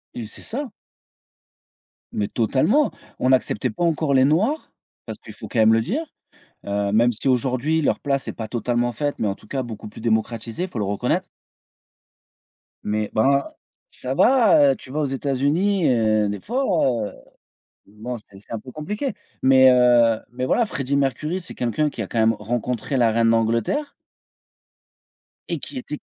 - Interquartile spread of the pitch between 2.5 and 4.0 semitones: No, average, 5.0 semitones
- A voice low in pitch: Yes, low, 125 Hz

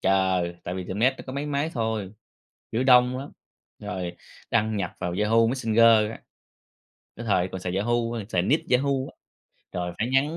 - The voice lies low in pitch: Yes, low, 110 Hz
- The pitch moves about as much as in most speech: Yes, average, 5.0 semitones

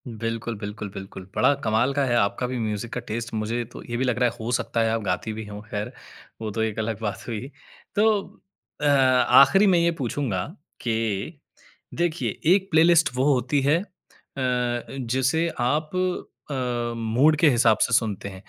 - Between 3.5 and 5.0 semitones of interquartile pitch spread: Yes, average, 3.9 semitones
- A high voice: No, low, 120 Hz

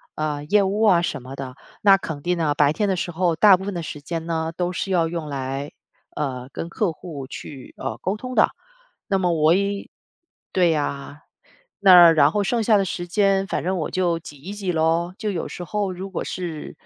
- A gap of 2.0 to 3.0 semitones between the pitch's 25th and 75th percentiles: No, average, 4.0 semitones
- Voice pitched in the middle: Yes, medium, 175 Hz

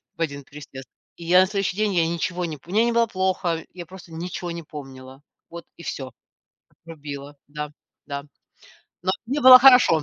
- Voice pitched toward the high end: No, medium, 170 Hz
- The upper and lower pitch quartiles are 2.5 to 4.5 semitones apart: Yes, average, 4.2 semitones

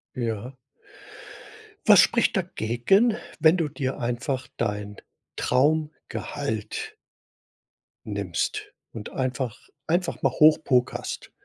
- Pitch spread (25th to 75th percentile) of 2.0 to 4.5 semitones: No, average, 5.2 semitones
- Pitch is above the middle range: No, low, 130 Hz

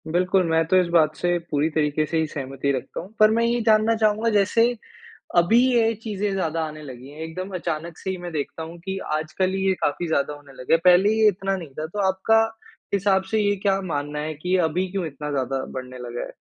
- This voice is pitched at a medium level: Yes, medium, 175 Hz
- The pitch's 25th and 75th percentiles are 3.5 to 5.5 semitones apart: Yes, average, 4.5 semitones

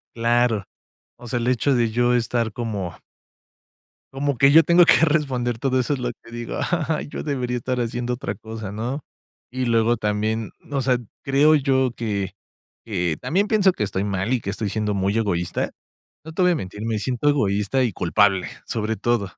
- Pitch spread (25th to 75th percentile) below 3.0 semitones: No, average, 4.0 semitones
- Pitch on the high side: No, low, 120 Hz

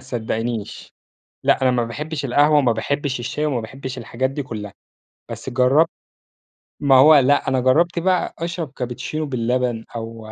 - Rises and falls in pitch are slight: No, average, 3.4 semitones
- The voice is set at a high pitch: No, low, 130 Hz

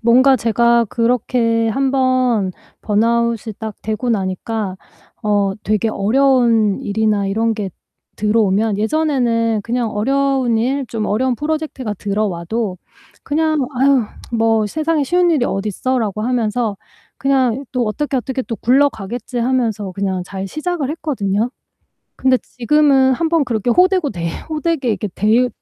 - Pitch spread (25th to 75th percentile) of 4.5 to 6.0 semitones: No, average, 3.9 semitones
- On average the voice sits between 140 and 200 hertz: No, high, 235 Hz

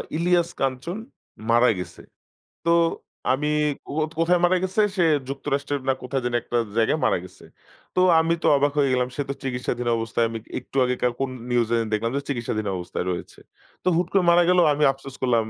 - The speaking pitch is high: No, low, 135 Hz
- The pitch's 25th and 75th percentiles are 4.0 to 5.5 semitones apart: Yes, average, 5.2 semitones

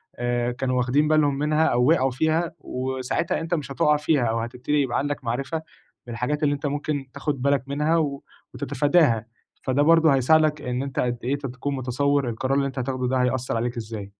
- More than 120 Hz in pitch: Yes, low, 135 Hz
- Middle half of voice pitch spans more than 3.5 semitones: No, average, 3.1 semitones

